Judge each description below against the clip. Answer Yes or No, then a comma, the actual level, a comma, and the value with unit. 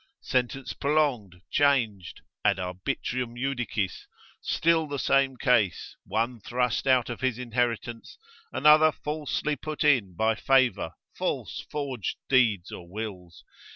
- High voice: No, low, 125 Hz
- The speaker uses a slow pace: Yes, slow, 120 wpm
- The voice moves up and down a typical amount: Yes, average, 4.2 semitones